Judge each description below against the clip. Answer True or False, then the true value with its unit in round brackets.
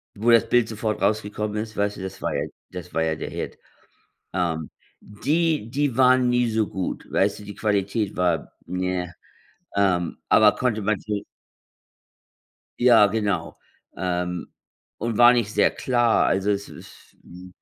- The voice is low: True (105 Hz)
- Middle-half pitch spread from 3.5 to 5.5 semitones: True (3.8 semitones)